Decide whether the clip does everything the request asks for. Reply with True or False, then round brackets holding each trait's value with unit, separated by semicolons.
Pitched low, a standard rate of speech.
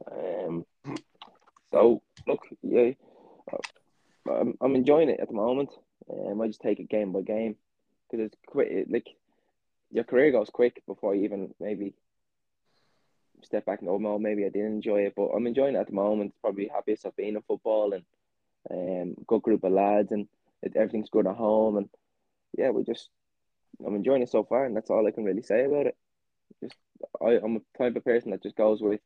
True (105 Hz; 195 wpm)